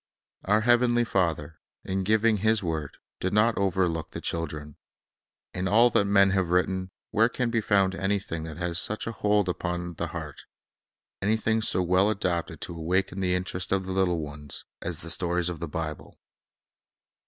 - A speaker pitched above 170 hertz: No, very low, 95 Hz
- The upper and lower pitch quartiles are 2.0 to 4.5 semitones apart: Yes, average, 3.5 semitones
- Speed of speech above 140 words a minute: Yes, average, 170 wpm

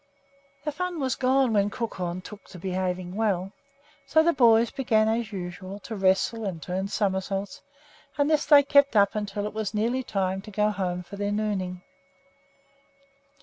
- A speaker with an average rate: Yes, average, 165 wpm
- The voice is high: Yes, high, 205 Hz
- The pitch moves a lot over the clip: No, average, 3.7 semitones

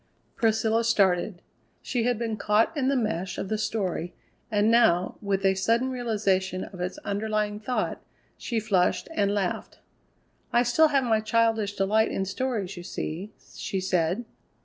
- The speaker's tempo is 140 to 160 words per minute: Yes, average, 155 wpm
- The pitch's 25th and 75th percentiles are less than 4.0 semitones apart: Yes, average, 3.1 semitones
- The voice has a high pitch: Yes, high, 215 Hz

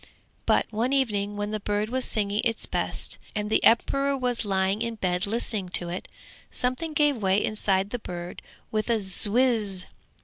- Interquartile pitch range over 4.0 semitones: No, average, 3.4 semitones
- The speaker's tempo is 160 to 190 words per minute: Yes, average, 170 wpm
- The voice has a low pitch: No, high, 215 Hz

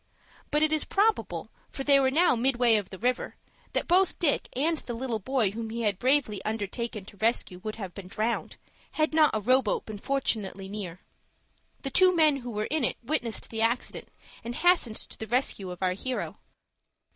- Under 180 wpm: No, average, 195 wpm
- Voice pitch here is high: Yes, high, 235 Hz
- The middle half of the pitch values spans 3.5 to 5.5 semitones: Yes, average, 4.7 semitones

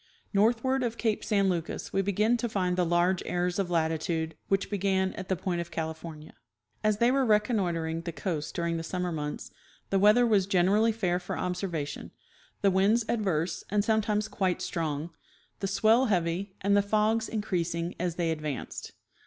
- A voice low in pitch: No, high, 190 Hz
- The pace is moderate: Yes, average, 180 wpm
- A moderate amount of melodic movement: Yes, average, 3.8 semitones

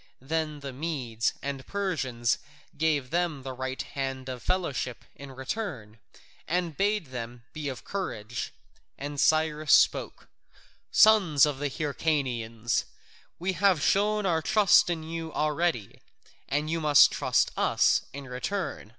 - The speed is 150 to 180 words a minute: No, slow, 135 wpm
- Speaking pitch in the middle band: Yes, medium, 150 Hz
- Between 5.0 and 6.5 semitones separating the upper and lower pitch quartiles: No, average, 4.6 semitones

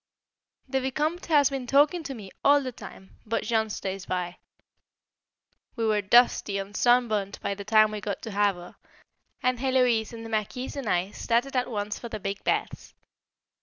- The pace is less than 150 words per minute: No, average, 180 wpm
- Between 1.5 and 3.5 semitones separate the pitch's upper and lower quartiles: No, average, 3.9 semitones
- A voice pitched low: No, high, 225 Hz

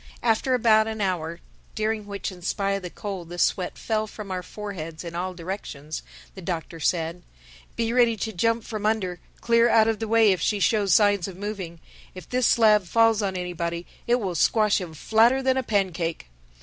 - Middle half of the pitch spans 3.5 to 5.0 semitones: Yes, average, 3.9 semitones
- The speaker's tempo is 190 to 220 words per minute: Yes, average, 195 wpm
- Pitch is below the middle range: No, high, 200 Hz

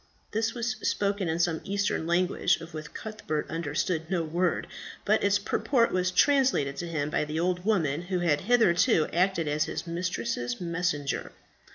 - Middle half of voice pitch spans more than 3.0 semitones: Yes, average, 4.1 semitones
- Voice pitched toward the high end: No, medium, 175 Hz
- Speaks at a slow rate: No, average, 165 wpm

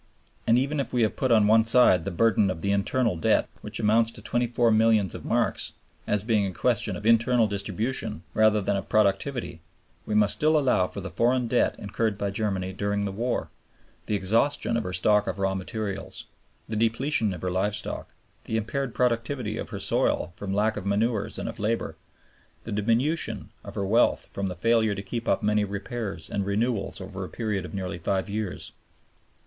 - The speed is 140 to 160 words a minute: No, average, 195 wpm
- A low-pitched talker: Yes, low, 105 Hz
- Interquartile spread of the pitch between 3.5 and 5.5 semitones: No, average, 2.8 semitones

